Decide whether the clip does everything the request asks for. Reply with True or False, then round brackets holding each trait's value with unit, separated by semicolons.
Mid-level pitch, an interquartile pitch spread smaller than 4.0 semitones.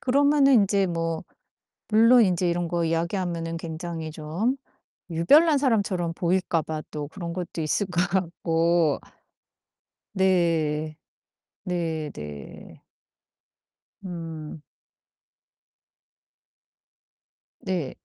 True (170 Hz; 2.7 semitones)